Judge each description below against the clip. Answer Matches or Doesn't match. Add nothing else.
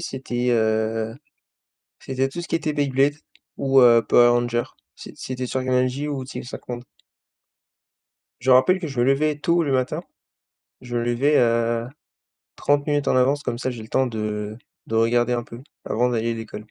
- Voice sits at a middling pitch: Doesn't match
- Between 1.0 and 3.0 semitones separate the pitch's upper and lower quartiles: Matches